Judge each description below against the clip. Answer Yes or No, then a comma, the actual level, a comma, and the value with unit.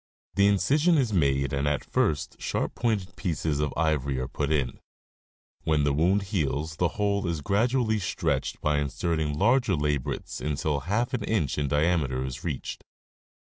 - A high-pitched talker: No, very low, 80 Hz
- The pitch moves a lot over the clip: Yes, wide, 5.8 semitones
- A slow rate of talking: No, average, 170 wpm